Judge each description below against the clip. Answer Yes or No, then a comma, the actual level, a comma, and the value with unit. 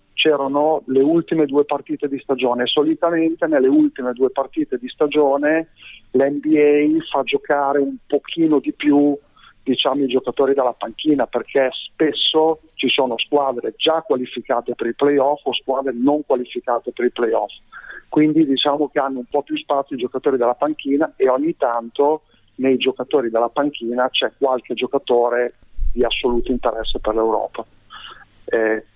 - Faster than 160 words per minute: No, average, 150 wpm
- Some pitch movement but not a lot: Yes, average, 3.2 semitones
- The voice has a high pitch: No, medium, 140 Hz